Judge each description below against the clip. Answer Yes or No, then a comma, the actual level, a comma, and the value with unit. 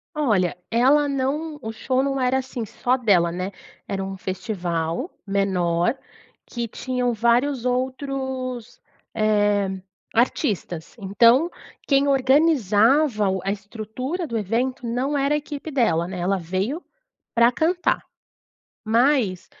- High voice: Yes, high, 235 Hz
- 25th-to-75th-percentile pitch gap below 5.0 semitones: No, wide, 5.4 semitones